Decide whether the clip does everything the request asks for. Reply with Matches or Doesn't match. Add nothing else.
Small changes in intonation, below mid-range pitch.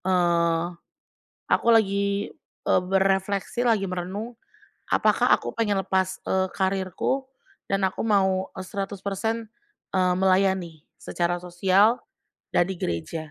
Doesn't match